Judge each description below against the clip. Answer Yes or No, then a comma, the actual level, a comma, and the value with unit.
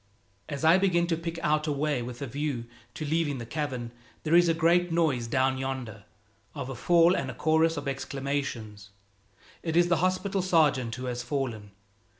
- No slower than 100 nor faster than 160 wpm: No, average, 185 wpm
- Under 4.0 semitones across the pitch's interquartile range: No, average, 4.5 semitones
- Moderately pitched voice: Yes, medium, 145 Hz